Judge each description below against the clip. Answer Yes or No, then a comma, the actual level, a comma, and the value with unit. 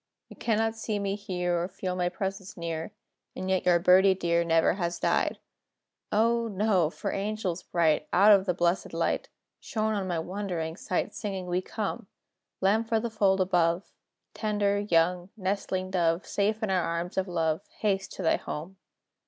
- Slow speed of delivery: No, average, 170 wpm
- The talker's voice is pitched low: No, high, 190 Hz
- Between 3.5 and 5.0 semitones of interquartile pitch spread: No, average, 2.9 semitones